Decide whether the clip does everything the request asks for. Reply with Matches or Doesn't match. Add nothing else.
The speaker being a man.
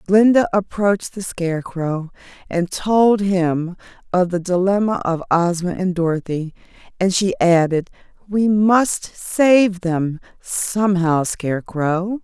Doesn't match